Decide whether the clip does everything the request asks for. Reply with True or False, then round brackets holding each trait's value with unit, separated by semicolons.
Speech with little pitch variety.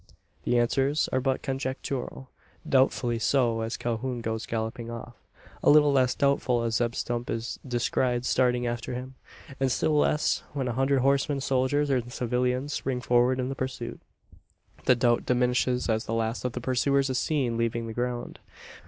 True (2.0 semitones)